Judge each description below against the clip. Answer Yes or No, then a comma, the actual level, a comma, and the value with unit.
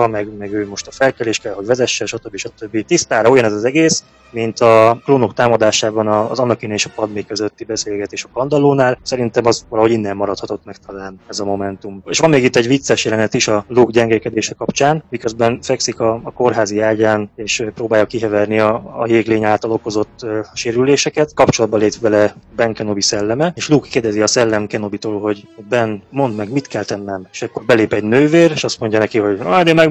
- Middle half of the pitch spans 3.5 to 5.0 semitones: No, average, 2.9 semitones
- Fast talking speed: Yes, fast, 200 wpm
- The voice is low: Yes, low, 110 Hz